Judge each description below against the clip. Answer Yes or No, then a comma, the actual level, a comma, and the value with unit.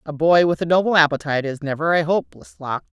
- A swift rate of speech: Yes, fast, 220 wpm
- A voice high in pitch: No, medium, 160 Hz